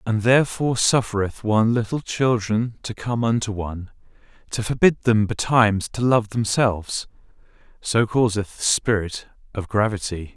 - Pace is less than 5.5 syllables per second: Yes, 4.8 syllables/s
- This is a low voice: Yes, low, 110 Hz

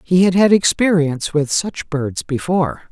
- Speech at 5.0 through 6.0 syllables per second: No, 4.7 syllables/s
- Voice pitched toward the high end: No, medium, 165 Hz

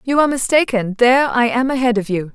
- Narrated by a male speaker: No, female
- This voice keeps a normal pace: No, fast, 230 wpm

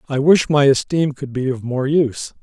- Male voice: Yes, male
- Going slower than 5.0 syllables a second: No, 5.1 syllables/s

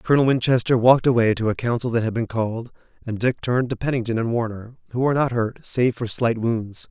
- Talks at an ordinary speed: No, fast, 225 wpm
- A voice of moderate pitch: No, low, 120 Hz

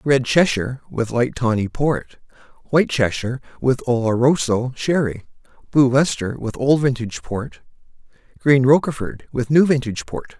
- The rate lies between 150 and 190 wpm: No, slow, 135 wpm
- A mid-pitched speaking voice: No, low, 130 Hz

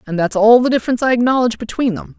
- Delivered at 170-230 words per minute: No, fast, 245 wpm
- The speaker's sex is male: No, female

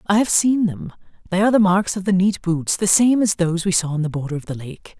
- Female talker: Yes, female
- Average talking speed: No, fast, 290 wpm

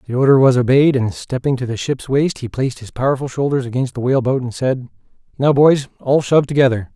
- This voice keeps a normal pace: No, fast, 225 wpm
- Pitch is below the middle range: Yes, low, 130 Hz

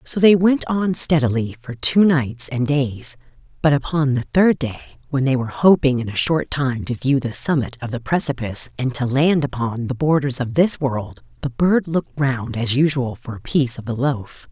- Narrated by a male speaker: No, female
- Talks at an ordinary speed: No, fast, 210 wpm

